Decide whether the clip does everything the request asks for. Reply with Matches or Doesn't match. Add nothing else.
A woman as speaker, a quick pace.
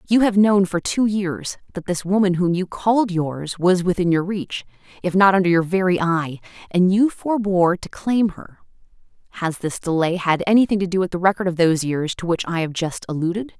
Matches